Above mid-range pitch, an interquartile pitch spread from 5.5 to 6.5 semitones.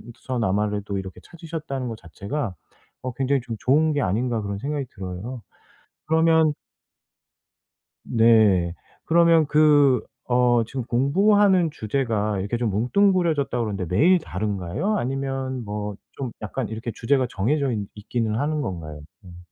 No: low, 125 Hz; wide, 6.0 semitones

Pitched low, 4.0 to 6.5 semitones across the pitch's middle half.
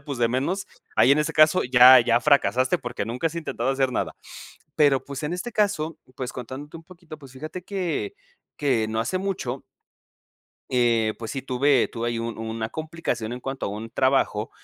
Yes: low, 130 Hz; average, 4.6 semitones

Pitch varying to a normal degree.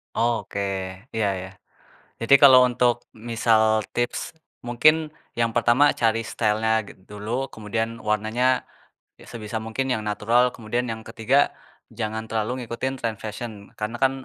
No: narrow, 1.9 semitones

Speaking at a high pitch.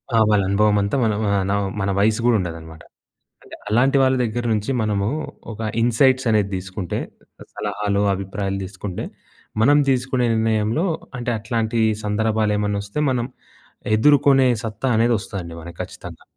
No: low, 105 Hz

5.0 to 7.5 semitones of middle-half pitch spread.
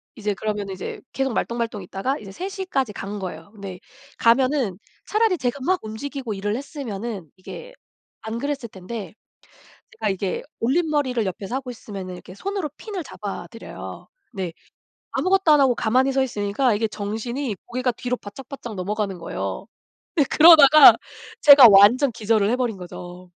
Yes: average, 5.3 semitones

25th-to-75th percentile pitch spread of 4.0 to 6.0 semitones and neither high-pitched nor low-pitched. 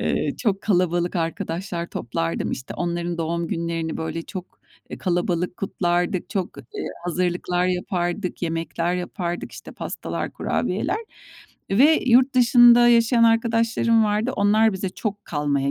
Yes: average, 4.6 semitones; medium, 180 Hz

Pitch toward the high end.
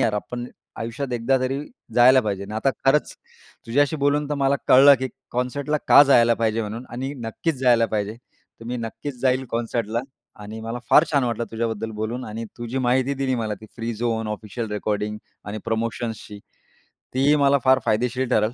No: low, 120 Hz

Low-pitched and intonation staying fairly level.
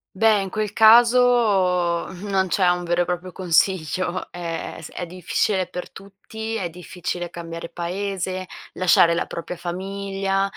No: medium, 185 Hz; narrow, 2.2 semitones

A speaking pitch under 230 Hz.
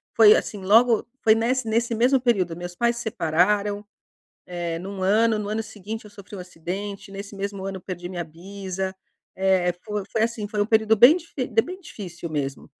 Yes: high, 205 Hz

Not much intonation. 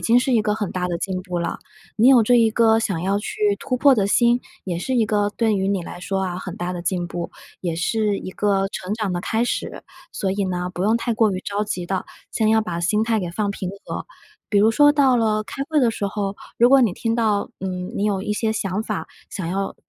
No: average, 3.4 semitones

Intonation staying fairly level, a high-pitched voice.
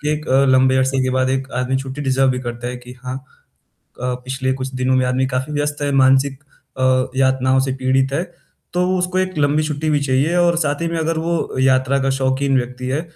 No: narrow, 2.0 semitones; low, 135 Hz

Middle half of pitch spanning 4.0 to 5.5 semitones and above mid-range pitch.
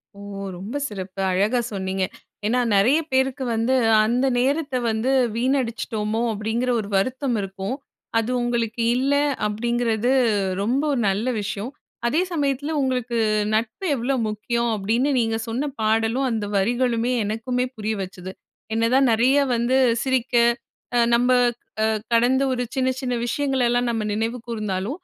No: average, 3.0 semitones; high, 235 Hz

